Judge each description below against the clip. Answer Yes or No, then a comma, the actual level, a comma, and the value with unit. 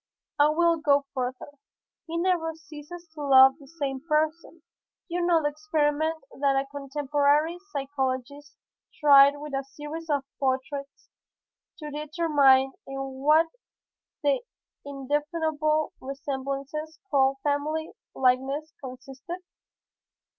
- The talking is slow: Yes, slow, 110 wpm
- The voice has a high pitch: Yes, very high, 290 Hz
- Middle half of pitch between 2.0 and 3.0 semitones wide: Yes, narrow, 2.4 semitones